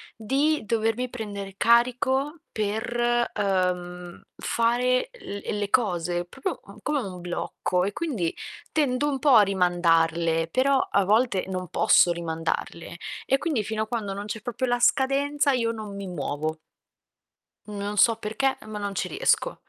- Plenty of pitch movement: Yes, wide, 5.7 semitones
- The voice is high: Yes, high, 215 Hz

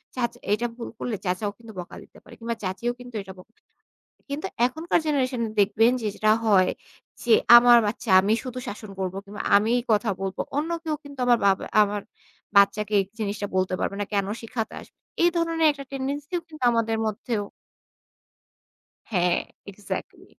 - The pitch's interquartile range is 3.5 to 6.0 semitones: Yes, average, 3.8 semitones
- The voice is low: No, high, 225 Hz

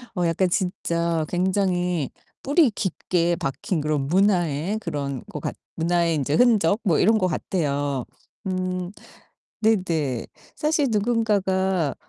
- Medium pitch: Yes, medium, 180 Hz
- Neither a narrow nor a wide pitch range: Yes, average, 3.9 semitones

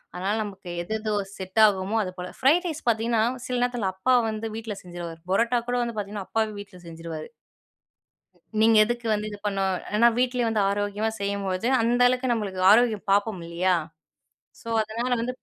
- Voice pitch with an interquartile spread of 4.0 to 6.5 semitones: No, average, 3.5 semitones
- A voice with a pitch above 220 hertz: No, high, 215 Hz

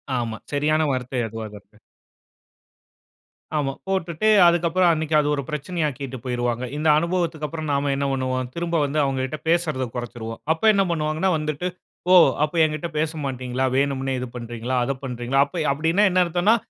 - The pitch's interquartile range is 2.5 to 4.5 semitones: Yes, average, 4.2 semitones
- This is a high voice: No, medium, 145 Hz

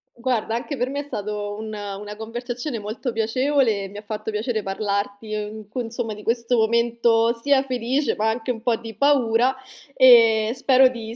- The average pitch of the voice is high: Yes, high, 230 Hz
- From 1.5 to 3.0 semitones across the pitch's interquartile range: Yes, narrow, 2.6 semitones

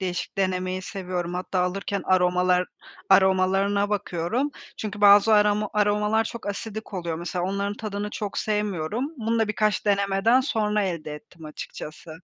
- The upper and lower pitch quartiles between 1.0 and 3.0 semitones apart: Yes, narrow, 2.5 semitones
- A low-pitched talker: No, high, 200 Hz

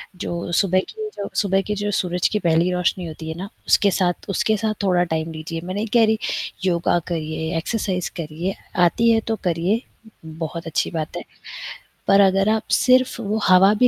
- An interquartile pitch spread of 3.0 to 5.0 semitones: Yes, average, 3.8 semitones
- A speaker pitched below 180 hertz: No, medium, 185 Hz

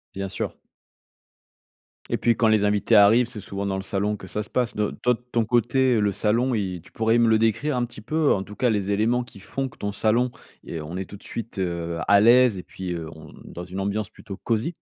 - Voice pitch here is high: No, low, 105 Hz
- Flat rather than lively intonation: No, average, 3.4 semitones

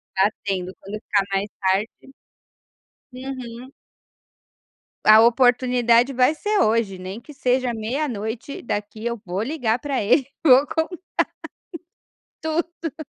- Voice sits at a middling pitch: No, high, 240 Hz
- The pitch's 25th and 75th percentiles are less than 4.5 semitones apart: Yes, average, 4.1 semitones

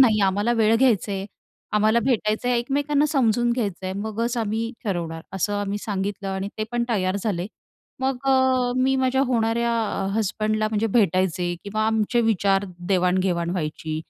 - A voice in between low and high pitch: No, high, 215 Hz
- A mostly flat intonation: No, average, 3.7 semitones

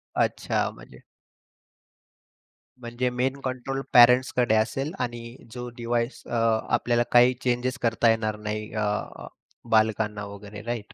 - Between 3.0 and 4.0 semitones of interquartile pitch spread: No, narrow, 2.4 semitones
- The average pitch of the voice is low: Yes, low, 120 Hz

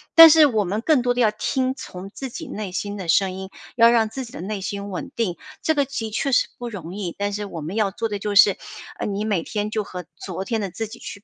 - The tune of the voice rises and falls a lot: No, average, 3.2 semitones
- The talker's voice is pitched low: No, high, 210 Hz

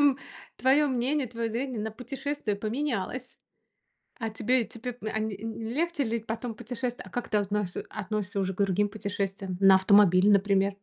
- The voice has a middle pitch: No, high, 220 Hz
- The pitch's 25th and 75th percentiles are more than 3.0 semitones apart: Yes, average, 3.7 semitones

